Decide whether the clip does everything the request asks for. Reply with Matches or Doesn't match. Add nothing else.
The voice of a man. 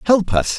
Matches